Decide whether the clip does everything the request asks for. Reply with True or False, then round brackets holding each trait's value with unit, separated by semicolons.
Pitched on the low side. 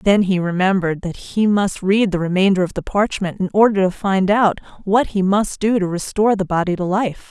False (195 Hz)